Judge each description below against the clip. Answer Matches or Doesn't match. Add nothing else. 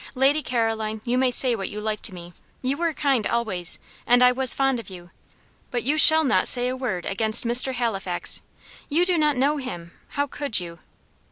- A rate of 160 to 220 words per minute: Matches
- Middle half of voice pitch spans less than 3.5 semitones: Doesn't match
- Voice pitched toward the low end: Doesn't match